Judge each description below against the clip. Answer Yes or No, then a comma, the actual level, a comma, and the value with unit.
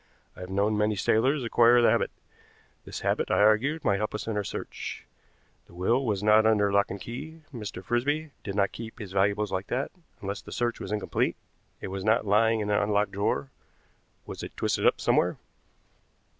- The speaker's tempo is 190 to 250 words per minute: Yes, average, 195 wpm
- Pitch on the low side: Yes, low, 105 Hz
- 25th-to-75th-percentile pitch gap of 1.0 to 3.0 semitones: Yes, average, 2.7 semitones